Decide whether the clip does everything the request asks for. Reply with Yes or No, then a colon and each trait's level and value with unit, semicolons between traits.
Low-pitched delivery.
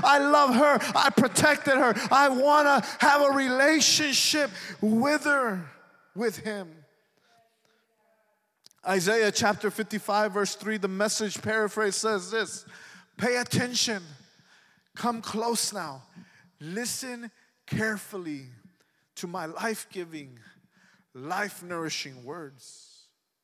No: high, 215 Hz